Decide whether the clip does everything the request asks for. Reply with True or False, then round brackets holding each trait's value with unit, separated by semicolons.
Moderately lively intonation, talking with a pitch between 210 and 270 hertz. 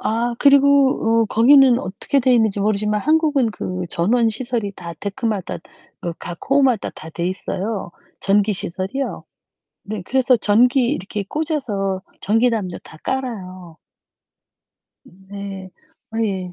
True (4.8 semitones; 215 Hz)